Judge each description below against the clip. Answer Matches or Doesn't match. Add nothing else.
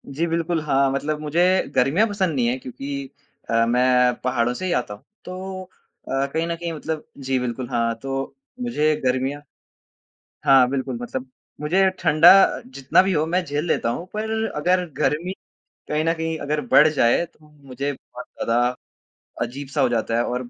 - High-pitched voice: Doesn't match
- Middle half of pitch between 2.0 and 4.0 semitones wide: Doesn't match